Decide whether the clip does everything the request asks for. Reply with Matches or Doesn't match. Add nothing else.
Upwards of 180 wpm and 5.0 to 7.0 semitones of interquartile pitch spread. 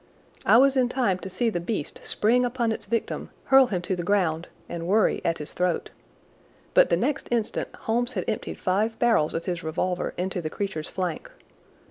Matches